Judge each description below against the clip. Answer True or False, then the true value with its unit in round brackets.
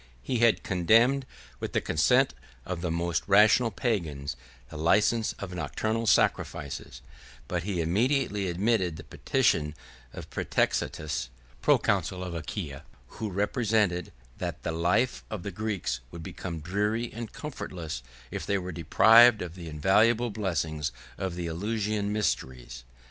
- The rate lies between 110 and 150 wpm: True (135 wpm)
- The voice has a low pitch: True (95 Hz)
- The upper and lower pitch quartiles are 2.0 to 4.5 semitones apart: False (4.9 semitones)